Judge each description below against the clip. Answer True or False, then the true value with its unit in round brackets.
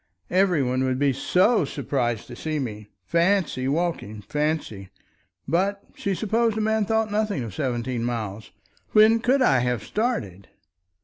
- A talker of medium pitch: True (150 Hz)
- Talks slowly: False (145 wpm)